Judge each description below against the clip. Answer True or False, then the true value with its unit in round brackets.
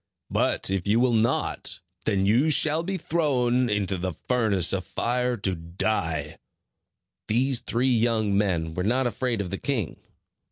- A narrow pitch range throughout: False (4.5 semitones)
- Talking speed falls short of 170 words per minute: True (155 wpm)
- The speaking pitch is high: False (110 Hz)